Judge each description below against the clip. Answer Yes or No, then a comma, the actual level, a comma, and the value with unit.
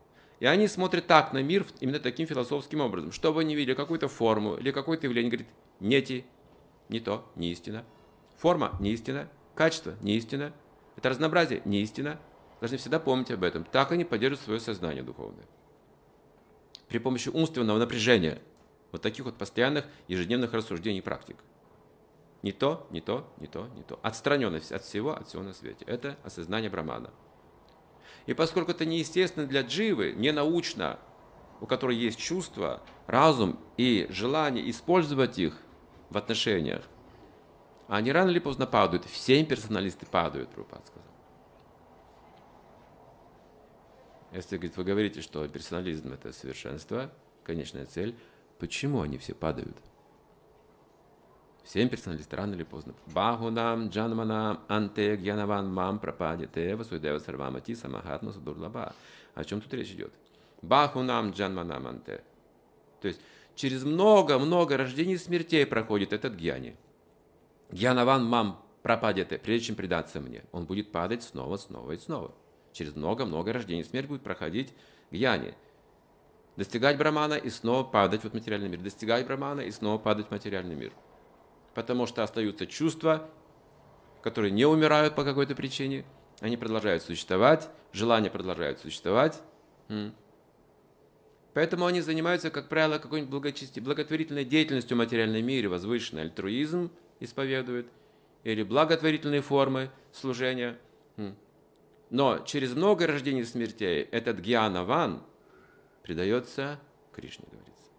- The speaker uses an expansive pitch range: Yes, wide, 5.7 semitones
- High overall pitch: No, low, 120 Hz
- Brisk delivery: No, average, 130 wpm